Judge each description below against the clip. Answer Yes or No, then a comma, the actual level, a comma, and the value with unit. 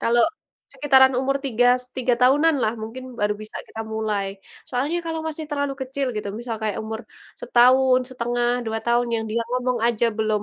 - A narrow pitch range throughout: No, average, 3.0 semitones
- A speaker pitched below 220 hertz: No, high, 245 Hz